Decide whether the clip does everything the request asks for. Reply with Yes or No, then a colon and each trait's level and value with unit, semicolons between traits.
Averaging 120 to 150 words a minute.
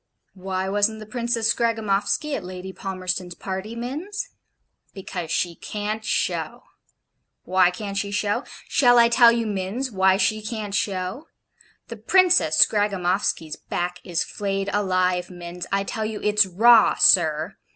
Yes: average, 140 wpm